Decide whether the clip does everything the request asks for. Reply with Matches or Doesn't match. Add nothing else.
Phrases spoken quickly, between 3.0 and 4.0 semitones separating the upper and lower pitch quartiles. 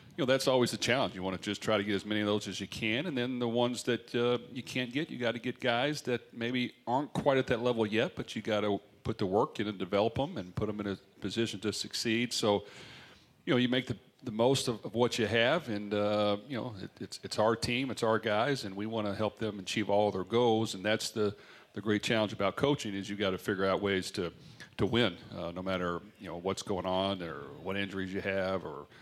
Matches